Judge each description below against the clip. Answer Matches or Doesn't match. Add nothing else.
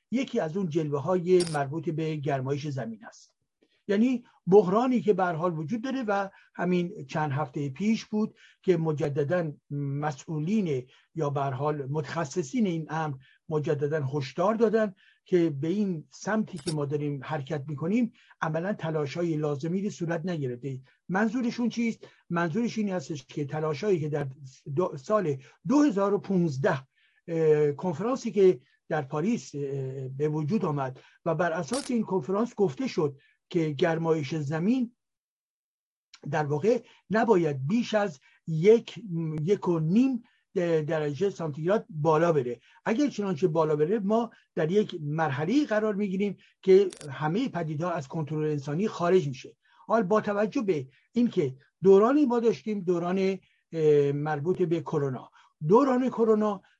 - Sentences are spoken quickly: Doesn't match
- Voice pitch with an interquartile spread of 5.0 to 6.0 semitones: Matches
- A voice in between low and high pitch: Matches